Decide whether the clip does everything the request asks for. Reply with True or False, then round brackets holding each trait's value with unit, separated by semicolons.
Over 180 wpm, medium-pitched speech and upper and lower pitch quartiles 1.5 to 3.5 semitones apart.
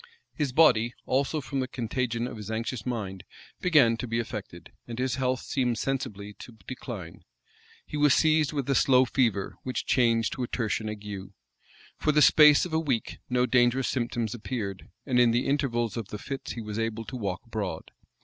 False (190 wpm; 120 Hz; 3.2 semitones)